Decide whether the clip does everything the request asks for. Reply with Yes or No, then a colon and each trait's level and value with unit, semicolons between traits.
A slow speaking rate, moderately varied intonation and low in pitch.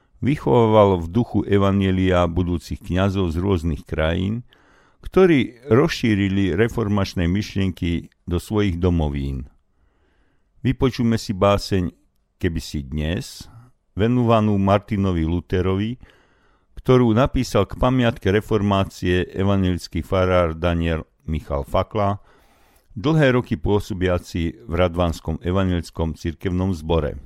Yes: slow, 95 wpm; average, 3.8 semitones; very low, 95 Hz